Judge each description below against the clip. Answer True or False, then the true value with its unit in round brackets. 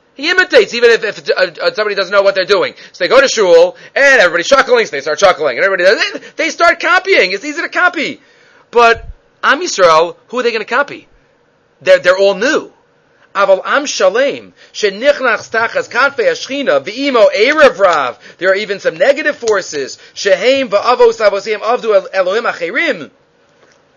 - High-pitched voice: True (290 Hz)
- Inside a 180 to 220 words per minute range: False (140 wpm)